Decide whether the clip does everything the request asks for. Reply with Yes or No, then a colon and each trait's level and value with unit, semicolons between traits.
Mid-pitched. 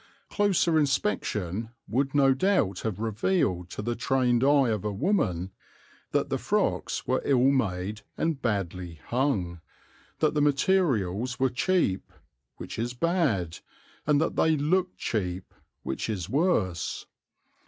No: low, 125 Hz